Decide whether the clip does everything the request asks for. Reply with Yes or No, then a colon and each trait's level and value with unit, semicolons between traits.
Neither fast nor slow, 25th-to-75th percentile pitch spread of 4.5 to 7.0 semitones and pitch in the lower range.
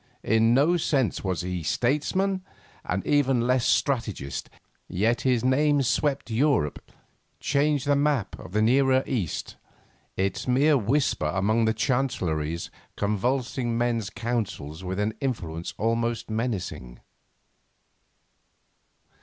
No: slow, 110 wpm; average, 5.2 semitones; low, 120 Hz